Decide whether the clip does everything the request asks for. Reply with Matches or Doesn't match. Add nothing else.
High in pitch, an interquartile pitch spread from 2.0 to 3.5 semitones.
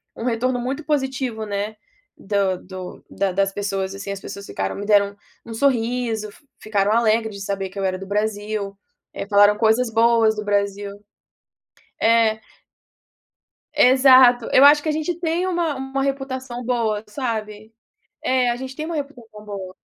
Doesn't match